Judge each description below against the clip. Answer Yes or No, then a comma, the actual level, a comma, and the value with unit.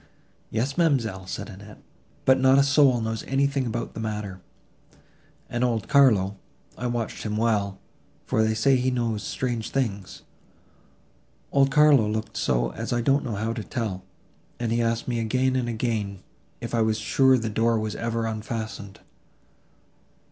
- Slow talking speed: No, average, 155 wpm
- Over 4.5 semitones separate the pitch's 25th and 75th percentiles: No, average, 3.2 semitones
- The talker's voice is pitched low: Yes, low, 115 Hz